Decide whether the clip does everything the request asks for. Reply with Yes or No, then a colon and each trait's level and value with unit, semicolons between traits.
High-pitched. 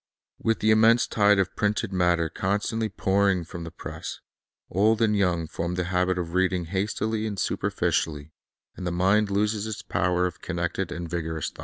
No: very low, 95 Hz